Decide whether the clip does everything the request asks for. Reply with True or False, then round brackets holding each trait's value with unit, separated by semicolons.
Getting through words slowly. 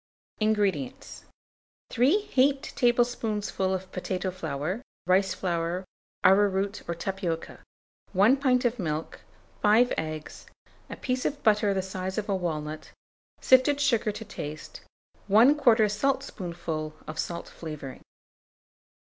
True (115 wpm)